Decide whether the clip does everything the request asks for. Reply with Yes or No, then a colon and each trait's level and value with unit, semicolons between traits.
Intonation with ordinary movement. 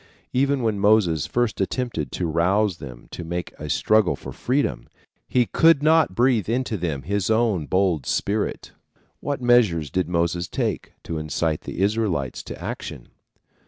No: wide, 6.2 semitones